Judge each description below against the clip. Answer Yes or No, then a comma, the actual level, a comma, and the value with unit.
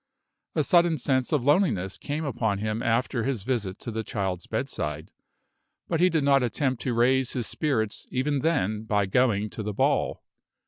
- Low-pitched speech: Yes, low, 120 Hz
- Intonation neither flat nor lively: Yes, average, 4.8 semitones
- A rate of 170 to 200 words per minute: Yes, average, 175 wpm